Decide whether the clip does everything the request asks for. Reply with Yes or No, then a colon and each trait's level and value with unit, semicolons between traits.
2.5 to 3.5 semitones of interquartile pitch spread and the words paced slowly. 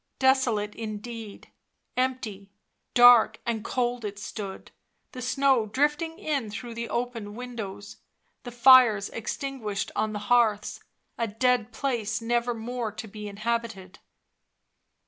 Yes: average, 2.8 semitones; slow, 120 wpm